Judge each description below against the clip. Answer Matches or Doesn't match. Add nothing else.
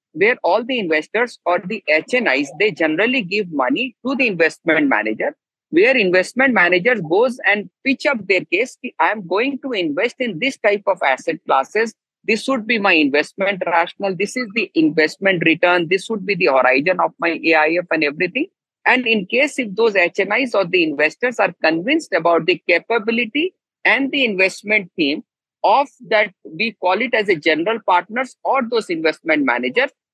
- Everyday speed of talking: Matches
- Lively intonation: Matches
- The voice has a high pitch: Matches